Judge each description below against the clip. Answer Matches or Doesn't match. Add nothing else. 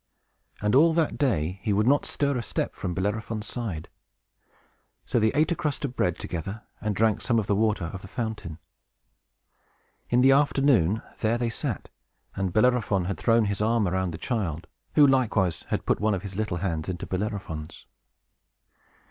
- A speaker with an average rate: Matches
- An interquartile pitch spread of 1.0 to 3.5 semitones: Doesn't match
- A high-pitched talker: Doesn't match